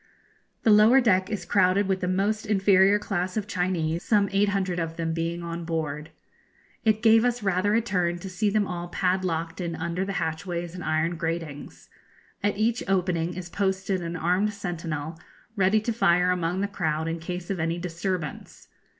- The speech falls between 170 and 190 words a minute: Yes, average, 180 wpm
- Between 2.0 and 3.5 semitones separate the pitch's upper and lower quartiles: Yes, average, 3.0 semitones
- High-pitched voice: No, medium, 180 Hz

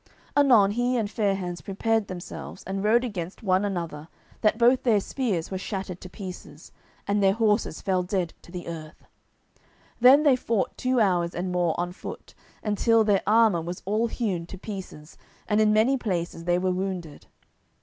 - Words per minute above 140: Yes, average, 175 wpm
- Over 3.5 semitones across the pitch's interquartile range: Yes, average, 3.9 semitones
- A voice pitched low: No, high, 195 Hz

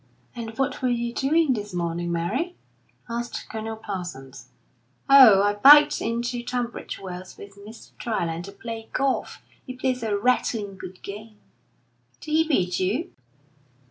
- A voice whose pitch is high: Yes, high, 225 Hz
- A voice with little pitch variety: No, average, 4.6 semitones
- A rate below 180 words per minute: Yes, average, 145 wpm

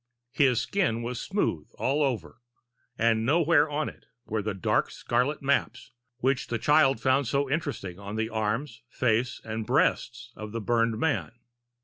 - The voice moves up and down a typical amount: Yes, average, 4.1 semitones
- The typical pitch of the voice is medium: No, low, 120 Hz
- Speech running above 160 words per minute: No, average, 155 wpm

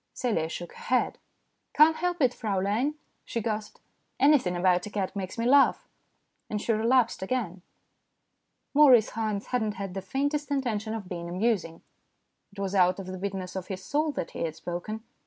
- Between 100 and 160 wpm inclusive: No, average, 185 wpm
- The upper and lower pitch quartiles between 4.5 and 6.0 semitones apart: Yes, average, 5.1 semitones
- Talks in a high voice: Yes, high, 210 Hz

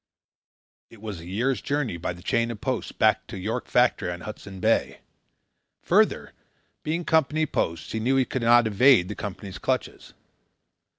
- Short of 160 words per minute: No, average, 165 wpm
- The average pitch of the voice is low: Yes, low, 110 Hz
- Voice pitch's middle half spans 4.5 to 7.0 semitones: Yes, average, 5.1 semitones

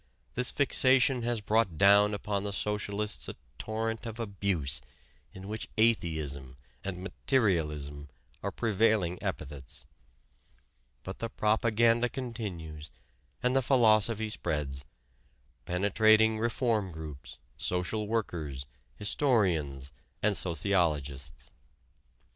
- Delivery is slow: Yes, slow, 95 wpm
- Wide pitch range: Yes, wide, 6.0 semitones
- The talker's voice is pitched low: Yes, low, 100 Hz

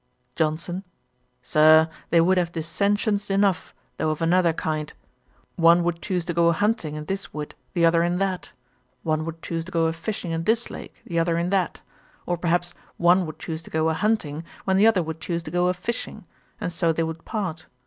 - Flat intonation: Yes, narrow, 2.3 semitones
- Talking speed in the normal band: No, fast, 210 wpm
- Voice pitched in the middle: Yes, medium, 170 Hz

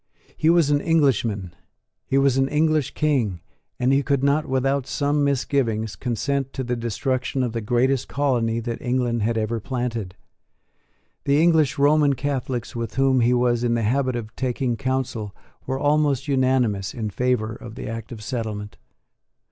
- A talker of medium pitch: No, low, 125 Hz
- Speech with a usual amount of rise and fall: Yes, average, 3.3 semitones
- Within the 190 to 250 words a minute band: No, average, 165 wpm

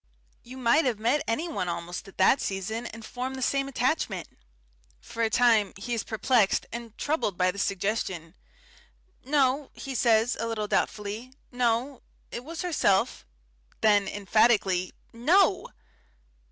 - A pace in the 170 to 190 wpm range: No, average, 140 wpm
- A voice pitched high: Yes, high, 230 Hz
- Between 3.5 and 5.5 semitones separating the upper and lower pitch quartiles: Yes, average, 4.3 semitones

